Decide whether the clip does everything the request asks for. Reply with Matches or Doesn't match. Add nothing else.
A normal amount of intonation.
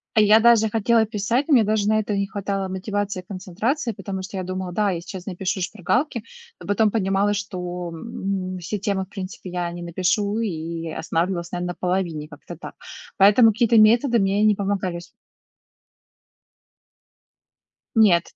Matches